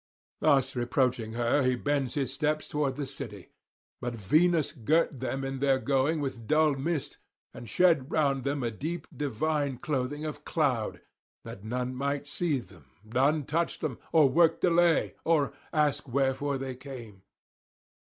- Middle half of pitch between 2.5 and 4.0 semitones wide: Yes, average, 3.1 semitones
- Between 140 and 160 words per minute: Yes, average, 155 wpm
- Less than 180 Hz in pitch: Yes, medium, 140 Hz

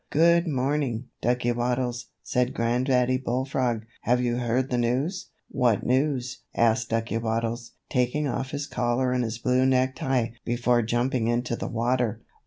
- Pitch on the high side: No, low, 125 Hz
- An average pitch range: No, narrow, 1.6 semitones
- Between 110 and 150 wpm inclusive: Yes, average, 145 wpm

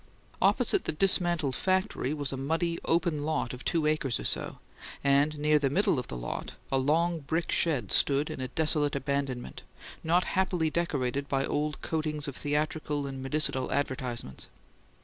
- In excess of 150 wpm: Yes, average, 165 wpm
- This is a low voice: No, medium, 150 Hz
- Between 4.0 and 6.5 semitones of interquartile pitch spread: No, average, 3.0 semitones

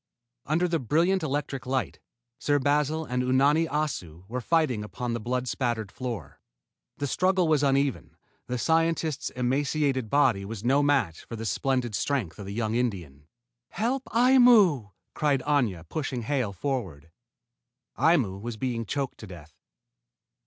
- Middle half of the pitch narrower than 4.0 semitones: No, average, 5.1 semitones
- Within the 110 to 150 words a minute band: Yes, average, 145 wpm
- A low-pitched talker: Yes, low, 130 Hz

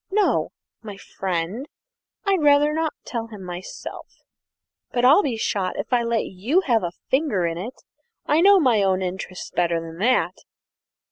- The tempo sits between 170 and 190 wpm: No, average, 160 wpm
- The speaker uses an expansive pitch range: Yes, wide, 7.7 semitones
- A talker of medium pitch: No, high, 225 Hz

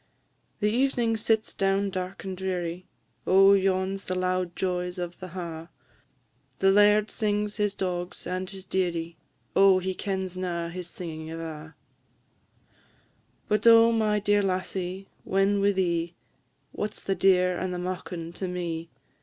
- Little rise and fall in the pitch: Yes, narrow, 1.9 semitones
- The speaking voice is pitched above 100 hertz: Yes, medium, 185 Hz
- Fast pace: No, average, 150 wpm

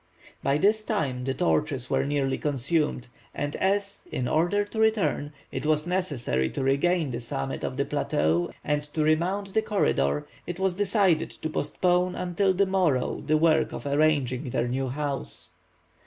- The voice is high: No, medium, 155 Hz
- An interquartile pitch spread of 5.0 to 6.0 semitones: Yes, wide, 5.6 semitones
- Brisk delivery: No, average, 165 wpm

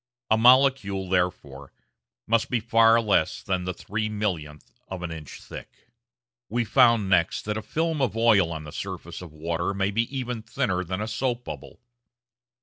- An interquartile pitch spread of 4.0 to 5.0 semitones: Yes, average, 4.5 semitones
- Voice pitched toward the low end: Yes, low, 105 Hz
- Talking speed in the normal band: Yes, average, 170 wpm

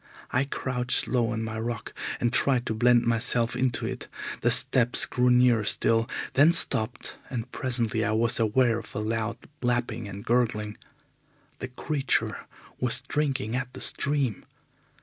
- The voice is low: Yes, low, 120 Hz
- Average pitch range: No, narrow, 2.1 semitones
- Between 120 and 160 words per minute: Yes, average, 150 wpm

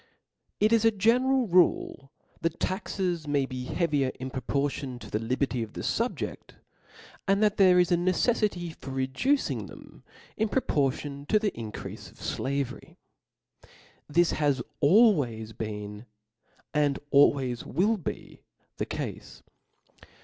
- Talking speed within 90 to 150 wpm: Yes, slow, 135 wpm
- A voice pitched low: No, medium, 150 Hz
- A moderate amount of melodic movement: No, wide, 7.0 semitones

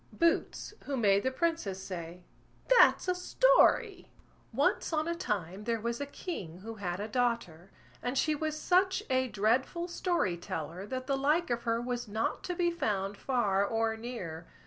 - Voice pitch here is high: Yes, high, 235 Hz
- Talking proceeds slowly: No, average, 170 wpm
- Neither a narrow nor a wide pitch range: No, wide, 8.1 semitones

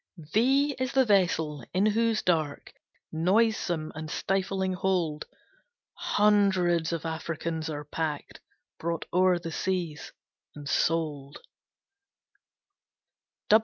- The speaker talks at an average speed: No, slow, 100 wpm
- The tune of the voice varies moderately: Yes, average, 3.8 semitones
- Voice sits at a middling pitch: Yes, medium, 170 Hz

